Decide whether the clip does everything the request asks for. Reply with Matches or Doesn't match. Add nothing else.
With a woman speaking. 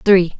Matches